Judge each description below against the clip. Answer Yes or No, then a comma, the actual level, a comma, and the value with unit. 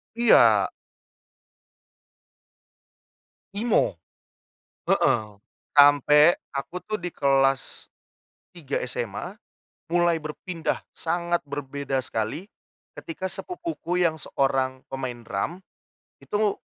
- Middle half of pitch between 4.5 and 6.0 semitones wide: Yes, average, 5.0 semitones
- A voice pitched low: No, medium, 150 Hz